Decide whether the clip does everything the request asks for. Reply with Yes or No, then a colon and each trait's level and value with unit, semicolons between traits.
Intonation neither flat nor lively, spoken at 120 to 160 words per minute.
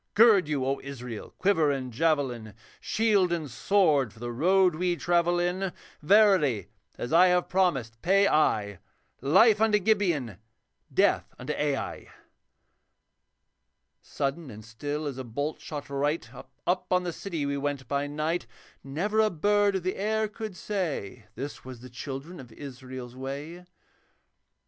No: wide, 5.8 semitones; average, 145 wpm